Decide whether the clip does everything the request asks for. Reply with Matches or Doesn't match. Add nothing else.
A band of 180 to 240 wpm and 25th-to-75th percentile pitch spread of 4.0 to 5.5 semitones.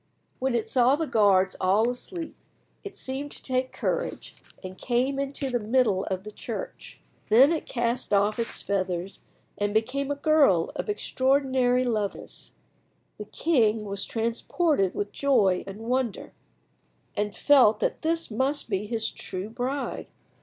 Doesn't match